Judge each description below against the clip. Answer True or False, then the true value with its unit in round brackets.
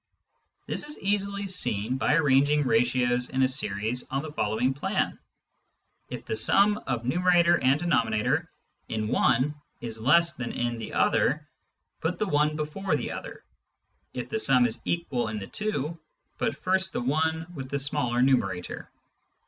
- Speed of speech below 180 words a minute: True (155 wpm)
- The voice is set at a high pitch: False (135 Hz)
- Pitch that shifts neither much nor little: False (5.8 semitones)